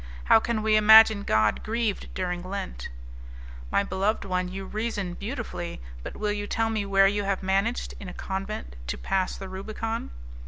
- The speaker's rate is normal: Yes, average, 170 wpm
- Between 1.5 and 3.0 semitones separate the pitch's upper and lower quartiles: Yes, narrow, 2.5 semitones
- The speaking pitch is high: Yes, high, 200 Hz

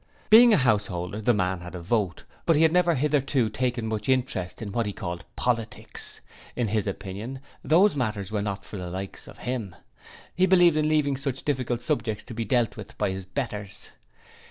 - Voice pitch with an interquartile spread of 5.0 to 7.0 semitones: Yes, wide, 5.4 semitones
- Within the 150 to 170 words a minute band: No, average, 195 wpm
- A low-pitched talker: Yes, low, 115 Hz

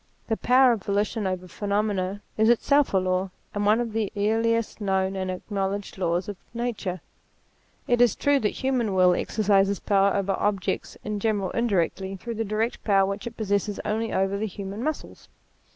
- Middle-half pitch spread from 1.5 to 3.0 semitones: Yes, narrow, 2.6 semitones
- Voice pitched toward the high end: Yes, high, 205 Hz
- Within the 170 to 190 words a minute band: Yes, average, 175 wpm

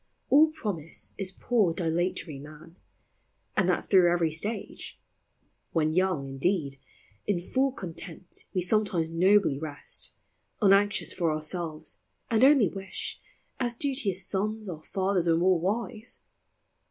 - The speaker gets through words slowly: Yes, slow, 130 wpm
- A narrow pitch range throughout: No, average, 4.0 semitones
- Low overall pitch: No, medium, 185 Hz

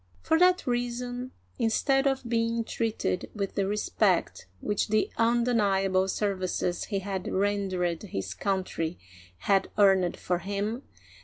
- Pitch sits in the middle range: No, high, 205 Hz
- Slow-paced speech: Yes, slow, 125 wpm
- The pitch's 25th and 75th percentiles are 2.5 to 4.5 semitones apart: Yes, average, 3.7 semitones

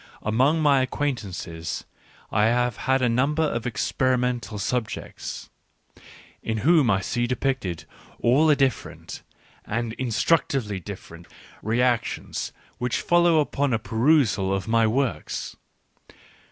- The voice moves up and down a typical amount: Yes, average, 4.0 semitones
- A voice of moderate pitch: No, low, 120 Hz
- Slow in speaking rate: Yes, slow, 110 wpm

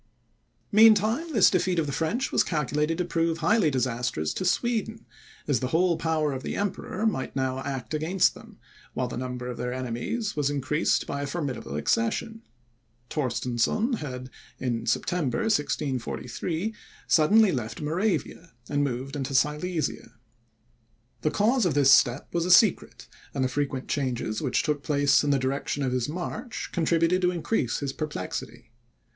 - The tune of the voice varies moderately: No, wide, 5.7 semitones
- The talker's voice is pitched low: No, medium, 150 Hz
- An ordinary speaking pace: Yes, average, 155 wpm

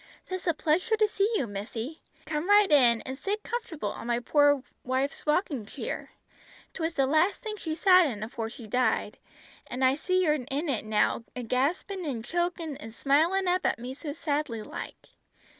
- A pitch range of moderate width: No, wide, 6.2 semitones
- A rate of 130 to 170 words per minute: No, average, 185 wpm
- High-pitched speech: Yes, very high, 295 Hz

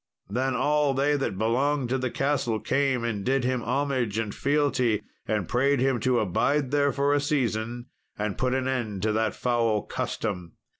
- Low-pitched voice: Yes, low, 125 Hz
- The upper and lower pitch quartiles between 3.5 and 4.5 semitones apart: Yes, average, 3.8 semitones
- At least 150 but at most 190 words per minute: Yes, average, 180 wpm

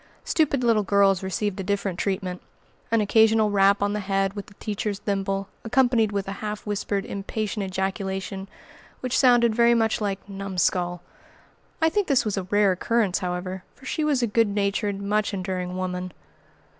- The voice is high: Yes, high, 200 Hz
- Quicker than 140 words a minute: Yes, average, 170 wpm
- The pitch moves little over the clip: Yes, narrow, 2.3 semitones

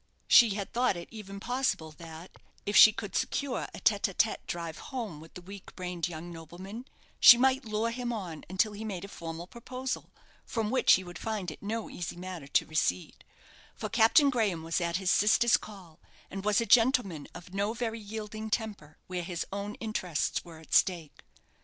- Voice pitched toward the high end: Yes, high, 200 Hz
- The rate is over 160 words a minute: Yes, average, 190 wpm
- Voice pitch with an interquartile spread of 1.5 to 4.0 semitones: No, average, 4.5 semitones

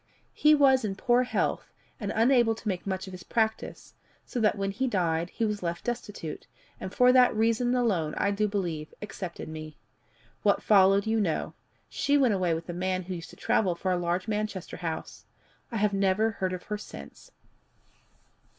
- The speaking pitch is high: Yes, high, 200 Hz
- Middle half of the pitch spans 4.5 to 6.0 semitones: No, average, 3.8 semitones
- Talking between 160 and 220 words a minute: Yes, average, 185 wpm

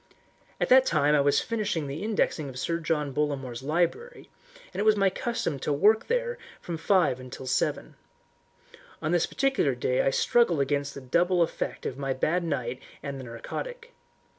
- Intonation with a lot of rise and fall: Yes, wide, 6.9 semitones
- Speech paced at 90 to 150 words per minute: No, average, 175 wpm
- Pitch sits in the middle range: Yes, medium, 155 Hz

